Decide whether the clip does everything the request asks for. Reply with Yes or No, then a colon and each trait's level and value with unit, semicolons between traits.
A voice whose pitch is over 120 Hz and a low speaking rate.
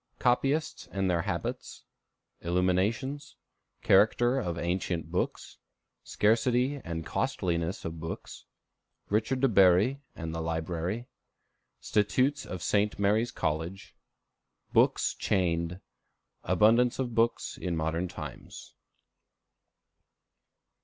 No: very low, 95 Hz; slow, 90 wpm